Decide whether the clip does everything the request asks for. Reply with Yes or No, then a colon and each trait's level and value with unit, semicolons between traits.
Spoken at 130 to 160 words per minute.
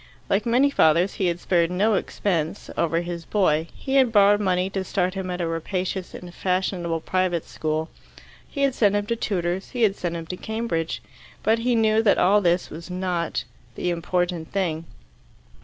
No: average, 185 wpm